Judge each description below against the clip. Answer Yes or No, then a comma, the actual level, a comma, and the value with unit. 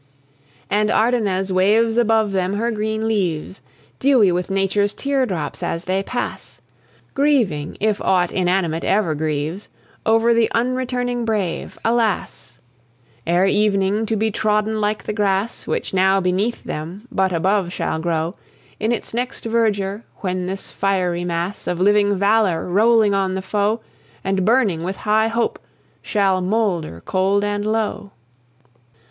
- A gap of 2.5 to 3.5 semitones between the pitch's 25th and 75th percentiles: Yes, average, 3.1 semitones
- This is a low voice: No, high, 200 Hz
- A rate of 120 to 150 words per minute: Yes, average, 140 wpm